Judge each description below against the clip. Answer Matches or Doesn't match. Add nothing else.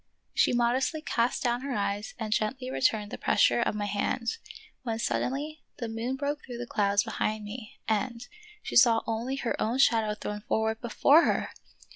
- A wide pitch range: Doesn't match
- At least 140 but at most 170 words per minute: Doesn't match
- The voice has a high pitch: Matches